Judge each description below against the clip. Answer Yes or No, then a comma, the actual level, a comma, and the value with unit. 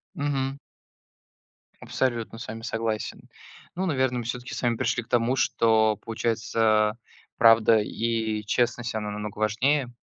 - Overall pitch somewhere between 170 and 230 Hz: No, low, 115 Hz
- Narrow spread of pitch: Yes, narrow, 2.1 semitones